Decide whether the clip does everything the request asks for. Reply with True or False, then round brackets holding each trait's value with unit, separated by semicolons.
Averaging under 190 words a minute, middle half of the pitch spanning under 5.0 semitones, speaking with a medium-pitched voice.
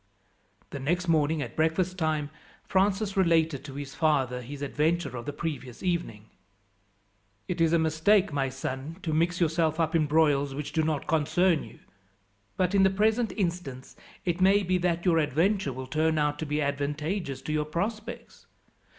True (170 wpm; 3.7 semitones; 160 Hz)